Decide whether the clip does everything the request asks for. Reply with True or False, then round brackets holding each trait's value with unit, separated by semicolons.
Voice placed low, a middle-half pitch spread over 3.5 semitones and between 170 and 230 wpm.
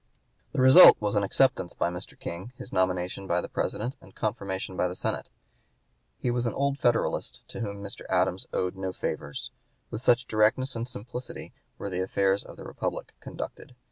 True (100 Hz; 4.7 semitones; 180 wpm)